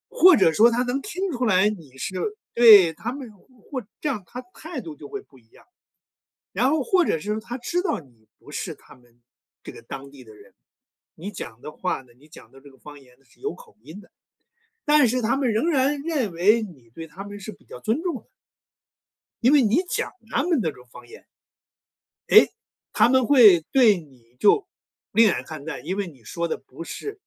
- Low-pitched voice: No, high, 205 Hz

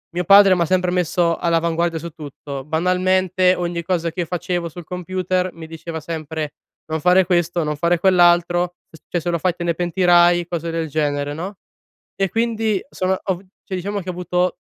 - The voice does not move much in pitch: Yes, narrow, 1.8 semitones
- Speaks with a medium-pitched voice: Yes, medium, 175 Hz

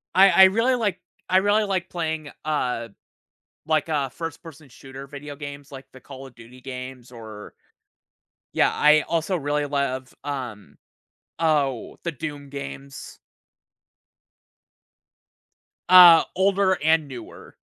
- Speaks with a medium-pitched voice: Yes, medium, 145 Hz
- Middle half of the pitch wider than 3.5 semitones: Yes, average, 4.1 semitones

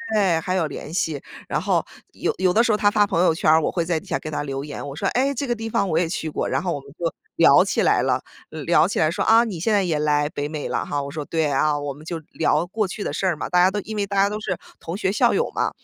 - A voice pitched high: No, medium, 170 Hz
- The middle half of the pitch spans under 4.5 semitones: No, average, 4.8 semitones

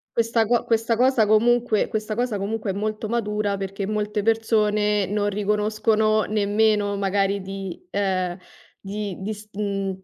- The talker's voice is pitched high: Yes, high, 210 Hz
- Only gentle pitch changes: Yes, narrow, 1.6 semitones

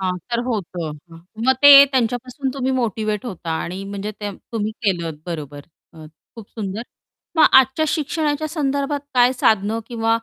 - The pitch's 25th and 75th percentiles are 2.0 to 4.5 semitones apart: No, average, 5.3 semitones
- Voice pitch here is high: Yes, high, 225 Hz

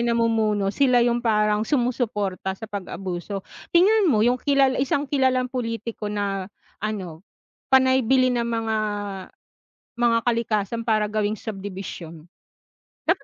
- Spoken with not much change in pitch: No, average, 3.5 semitones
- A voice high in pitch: Yes, high, 225 Hz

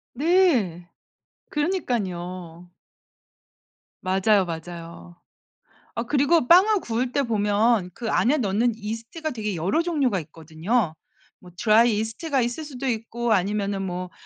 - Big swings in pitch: Yes, wide, 5.8 semitones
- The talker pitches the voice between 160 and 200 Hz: No, high, 220 Hz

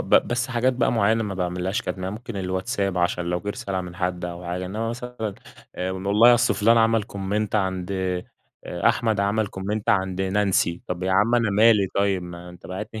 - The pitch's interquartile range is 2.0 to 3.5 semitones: Yes, average, 3.2 semitones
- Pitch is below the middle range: Yes, low, 100 Hz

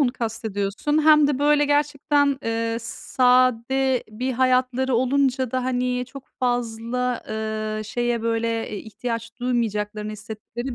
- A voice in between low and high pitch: No, high, 245 Hz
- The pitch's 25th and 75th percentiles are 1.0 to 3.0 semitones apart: Yes, narrow, 2.5 semitones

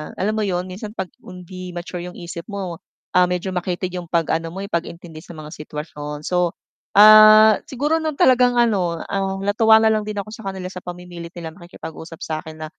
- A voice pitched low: No, medium, 180 Hz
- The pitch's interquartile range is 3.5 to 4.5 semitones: Yes, average, 3.8 semitones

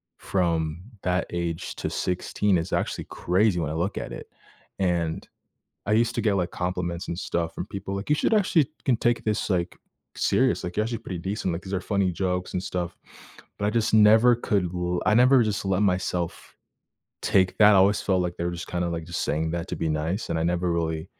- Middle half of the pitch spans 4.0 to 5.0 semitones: No, average, 3.2 semitones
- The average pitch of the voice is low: Yes, very low, 90 Hz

